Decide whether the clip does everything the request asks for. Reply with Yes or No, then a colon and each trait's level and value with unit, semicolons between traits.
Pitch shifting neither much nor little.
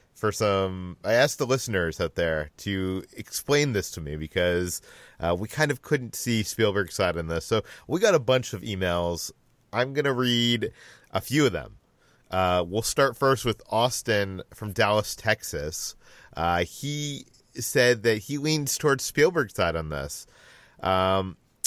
No: wide, 6.5 semitones